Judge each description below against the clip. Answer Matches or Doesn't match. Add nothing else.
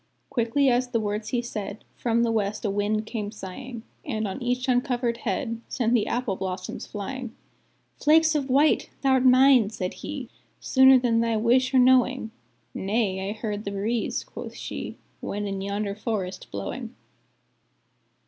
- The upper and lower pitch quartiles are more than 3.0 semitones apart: Matches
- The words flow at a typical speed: Matches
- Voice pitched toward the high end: Matches